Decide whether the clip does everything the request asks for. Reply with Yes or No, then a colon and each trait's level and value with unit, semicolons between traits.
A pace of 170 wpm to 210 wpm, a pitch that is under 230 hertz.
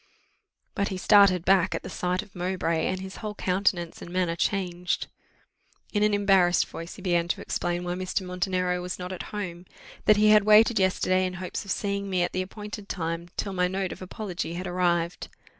Yes: average, 200 wpm; medium, 185 Hz